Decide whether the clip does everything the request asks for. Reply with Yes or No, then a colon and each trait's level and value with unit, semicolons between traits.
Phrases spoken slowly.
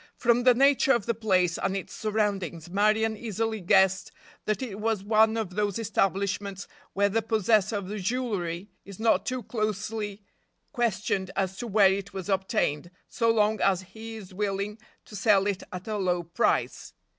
No: average, 170 wpm